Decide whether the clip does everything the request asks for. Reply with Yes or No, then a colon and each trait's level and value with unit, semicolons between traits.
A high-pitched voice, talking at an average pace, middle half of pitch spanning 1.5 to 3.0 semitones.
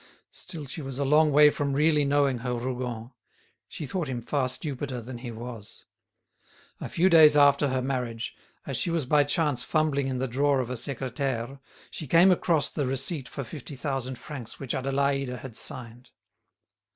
No: low, 135 Hz; average, 175 wpm; average, 2.7 semitones